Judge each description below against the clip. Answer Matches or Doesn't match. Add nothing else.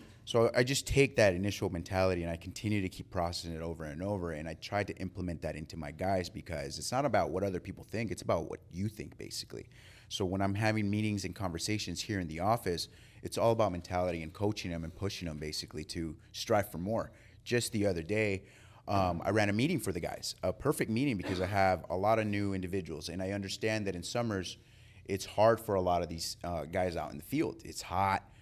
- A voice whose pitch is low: Matches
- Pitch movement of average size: Matches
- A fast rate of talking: Matches